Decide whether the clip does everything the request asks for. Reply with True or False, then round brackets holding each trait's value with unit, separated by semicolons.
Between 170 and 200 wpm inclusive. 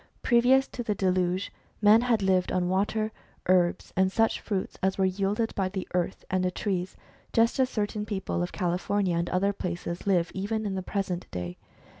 True (185 wpm)